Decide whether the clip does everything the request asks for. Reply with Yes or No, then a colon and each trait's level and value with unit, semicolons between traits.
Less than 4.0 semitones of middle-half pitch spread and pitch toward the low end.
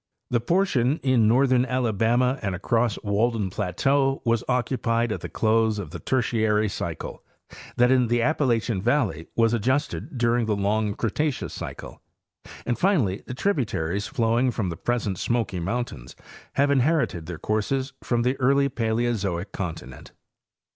Yes: average, 3.6 semitones; low, 115 Hz